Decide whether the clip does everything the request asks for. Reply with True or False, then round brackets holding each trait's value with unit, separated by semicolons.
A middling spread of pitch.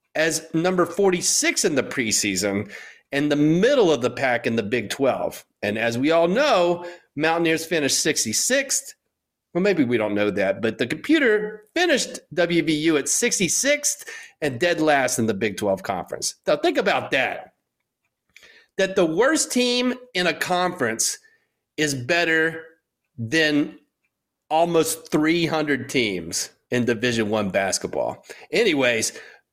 False (6.0 semitones)